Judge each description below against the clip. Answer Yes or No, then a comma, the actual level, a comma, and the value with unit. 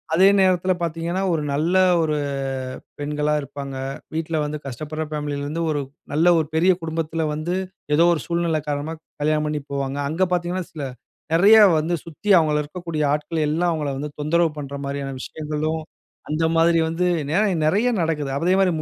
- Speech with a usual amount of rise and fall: No, narrow, 2.3 semitones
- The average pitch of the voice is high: No, medium, 160 Hz